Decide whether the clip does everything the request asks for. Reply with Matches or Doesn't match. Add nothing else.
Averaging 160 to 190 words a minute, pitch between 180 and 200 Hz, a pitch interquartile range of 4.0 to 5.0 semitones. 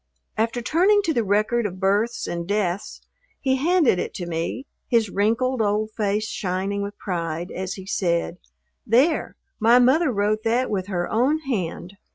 Doesn't match